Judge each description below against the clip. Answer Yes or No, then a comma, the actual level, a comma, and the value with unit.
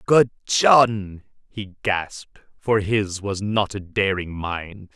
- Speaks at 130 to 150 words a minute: Yes, slow, 135 wpm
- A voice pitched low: Yes, low, 100 Hz